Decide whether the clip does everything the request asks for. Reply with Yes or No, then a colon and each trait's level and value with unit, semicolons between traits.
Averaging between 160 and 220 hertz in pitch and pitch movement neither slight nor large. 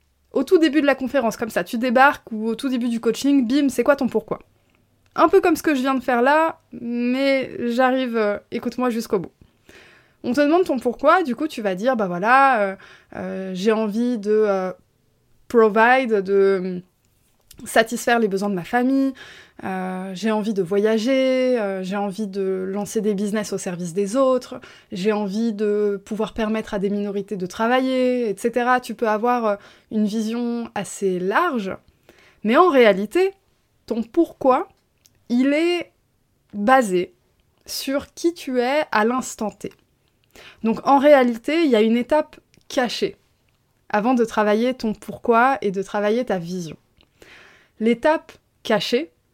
No: high, 230 Hz; average, 4.1 semitones